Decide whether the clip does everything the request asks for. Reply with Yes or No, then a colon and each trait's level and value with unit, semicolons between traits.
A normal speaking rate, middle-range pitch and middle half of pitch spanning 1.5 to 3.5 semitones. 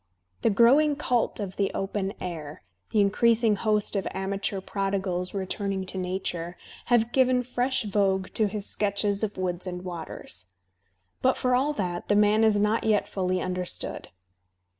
No: average, 155 wpm; high, 200 Hz; average, 2.9 semitones